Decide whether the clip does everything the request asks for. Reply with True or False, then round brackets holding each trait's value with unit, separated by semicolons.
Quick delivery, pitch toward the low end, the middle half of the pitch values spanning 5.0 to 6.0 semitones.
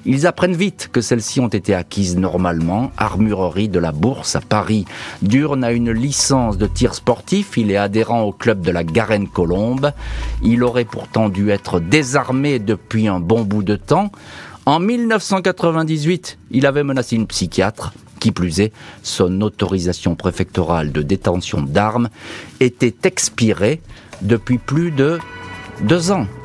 False (145 wpm; 110 Hz; 5.4 semitones)